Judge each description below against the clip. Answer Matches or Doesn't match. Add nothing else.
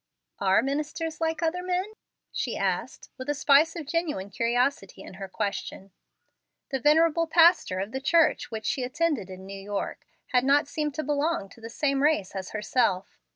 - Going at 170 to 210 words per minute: Matches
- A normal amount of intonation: Doesn't match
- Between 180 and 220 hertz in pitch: Doesn't match